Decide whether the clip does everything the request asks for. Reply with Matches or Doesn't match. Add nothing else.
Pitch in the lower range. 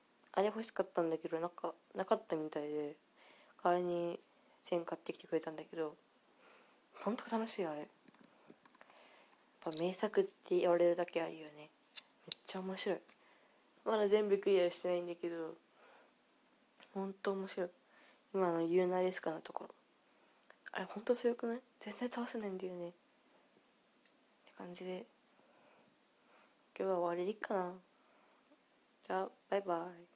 Doesn't match